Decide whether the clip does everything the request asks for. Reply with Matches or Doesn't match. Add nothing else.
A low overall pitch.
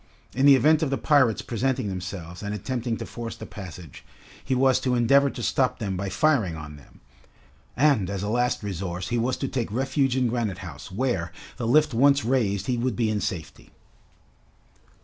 Matches